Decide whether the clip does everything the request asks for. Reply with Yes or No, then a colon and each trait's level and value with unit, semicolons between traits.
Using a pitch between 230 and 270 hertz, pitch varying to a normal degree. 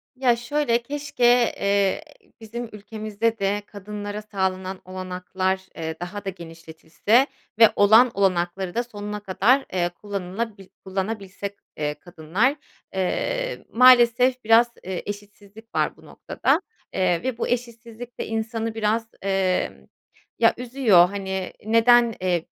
No: high, 210 Hz; average, 3.8 semitones